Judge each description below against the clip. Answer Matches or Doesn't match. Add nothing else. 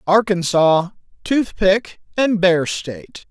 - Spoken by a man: Matches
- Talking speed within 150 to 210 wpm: Doesn't match